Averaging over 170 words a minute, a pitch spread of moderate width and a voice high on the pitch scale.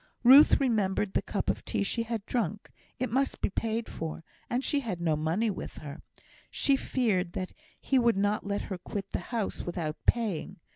Yes: average, 195 wpm; average, 4.5 semitones; high, 210 Hz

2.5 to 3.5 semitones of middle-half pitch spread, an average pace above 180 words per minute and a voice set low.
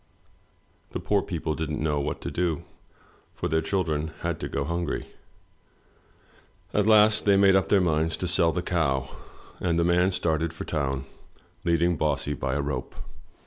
No: average, 3.0 semitones; average, 165 wpm; very low, 80 Hz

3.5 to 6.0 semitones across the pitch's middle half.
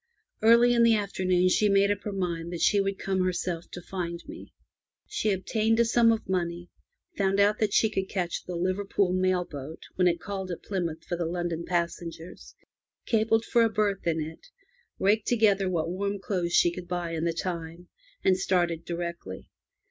No: average, 2.9 semitones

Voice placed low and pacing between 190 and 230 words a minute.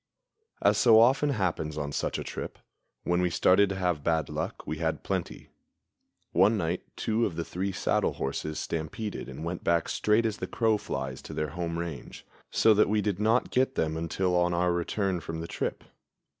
Yes: very low, 90 Hz; average, 195 wpm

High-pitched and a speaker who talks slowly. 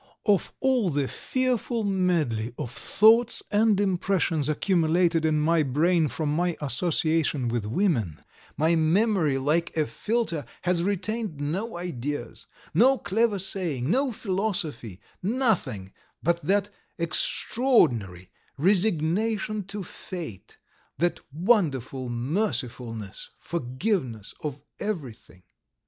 No: medium, 170 Hz; slow, 105 wpm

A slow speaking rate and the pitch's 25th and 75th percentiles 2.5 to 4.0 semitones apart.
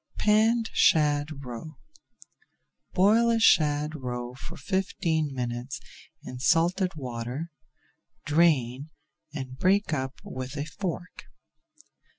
No: slow, 100 wpm; wide, 5.4 semitones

